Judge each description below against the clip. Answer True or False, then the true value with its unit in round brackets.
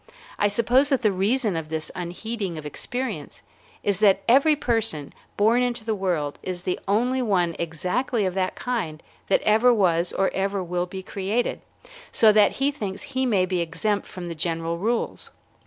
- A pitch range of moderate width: True (4.9 semitones)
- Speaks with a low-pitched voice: False (200 Hz)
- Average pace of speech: True (175 wpm)